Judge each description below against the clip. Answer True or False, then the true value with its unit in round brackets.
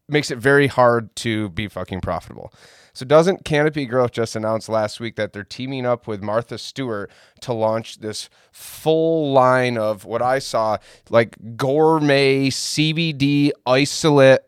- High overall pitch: False (125 Hz)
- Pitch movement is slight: False (4.3 semitones)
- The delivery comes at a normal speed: True (150 wpm)